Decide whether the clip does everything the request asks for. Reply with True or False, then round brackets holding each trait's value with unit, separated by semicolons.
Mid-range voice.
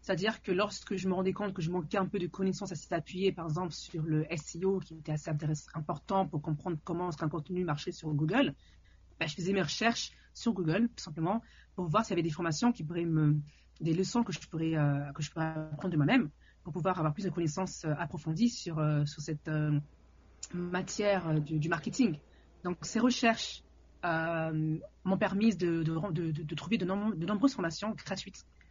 True (170 Hz)